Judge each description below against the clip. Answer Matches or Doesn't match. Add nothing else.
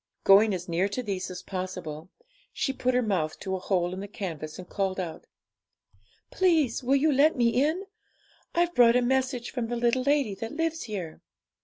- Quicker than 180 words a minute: Matches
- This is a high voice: Matches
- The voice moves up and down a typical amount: Doesn't match